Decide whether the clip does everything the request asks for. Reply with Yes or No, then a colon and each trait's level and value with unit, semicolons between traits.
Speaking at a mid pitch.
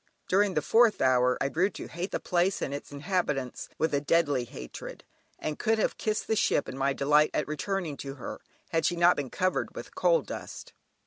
Yes: medium, 155 Hz